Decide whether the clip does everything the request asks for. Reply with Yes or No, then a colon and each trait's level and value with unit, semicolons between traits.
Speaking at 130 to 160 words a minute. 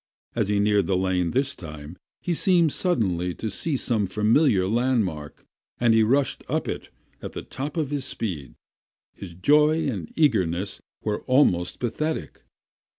Yes: average, 150 wpm